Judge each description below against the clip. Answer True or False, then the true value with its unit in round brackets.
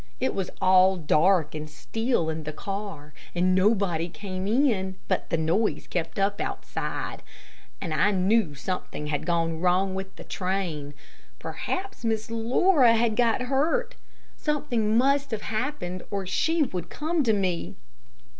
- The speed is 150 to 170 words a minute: True (155 wpm)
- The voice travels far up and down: False (4.8 semitones)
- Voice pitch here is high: True (195 Hz)